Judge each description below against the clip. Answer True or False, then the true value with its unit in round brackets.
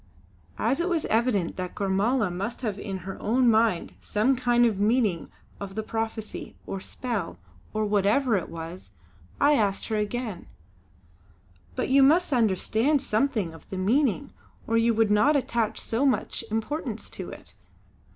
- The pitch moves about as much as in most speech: True (4.1 semitones)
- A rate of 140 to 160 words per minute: True (155 wpm)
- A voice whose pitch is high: True (220 Hz)